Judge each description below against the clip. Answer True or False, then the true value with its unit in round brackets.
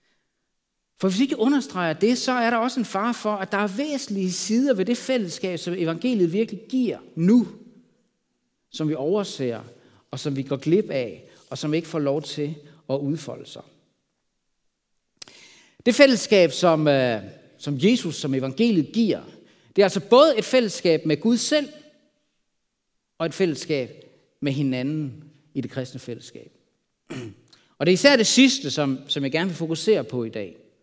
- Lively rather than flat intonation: True (8.0 semitones)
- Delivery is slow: False (165 wpm)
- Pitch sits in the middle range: True (175 Hz)